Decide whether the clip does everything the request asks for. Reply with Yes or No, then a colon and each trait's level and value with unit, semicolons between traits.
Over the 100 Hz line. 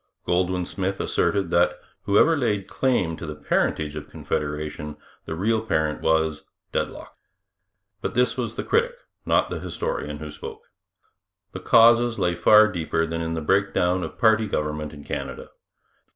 No: very low, 90 Hz